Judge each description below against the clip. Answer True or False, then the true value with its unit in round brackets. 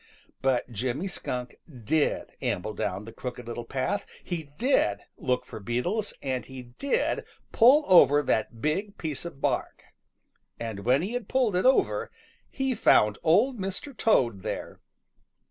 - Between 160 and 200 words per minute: False (145 wpm)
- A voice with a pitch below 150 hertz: True (140 Hz)